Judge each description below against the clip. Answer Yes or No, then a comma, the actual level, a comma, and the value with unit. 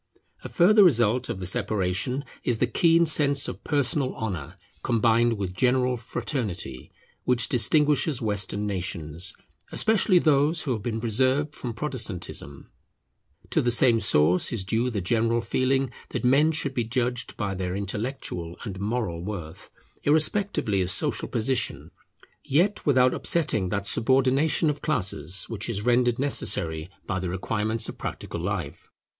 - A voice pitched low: Yes, low, 115 Hz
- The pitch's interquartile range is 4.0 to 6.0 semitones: Yes, wide, 5.4 semitones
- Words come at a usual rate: Yes, average, 145 wpm